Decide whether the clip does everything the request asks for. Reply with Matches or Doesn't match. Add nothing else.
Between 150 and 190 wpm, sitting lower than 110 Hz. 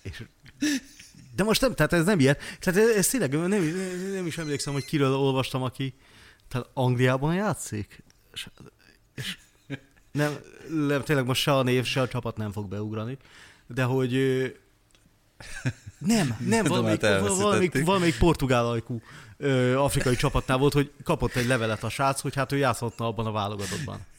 Doesn't match